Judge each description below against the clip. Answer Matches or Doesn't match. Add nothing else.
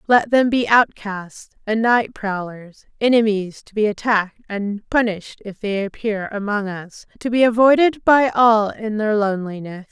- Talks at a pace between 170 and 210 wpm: Doesn't match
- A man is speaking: Doesn't match